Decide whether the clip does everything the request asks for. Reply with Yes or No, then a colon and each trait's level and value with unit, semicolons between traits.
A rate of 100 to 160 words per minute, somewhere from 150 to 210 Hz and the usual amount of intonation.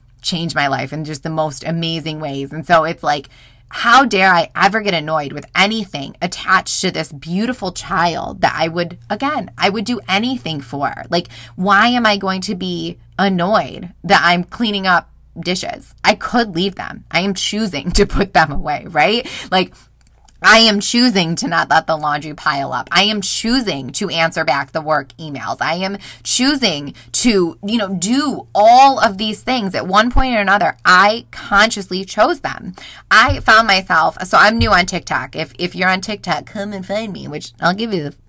No: average, 190 wpm; medium, 185 Hz; average, 5.0 semitones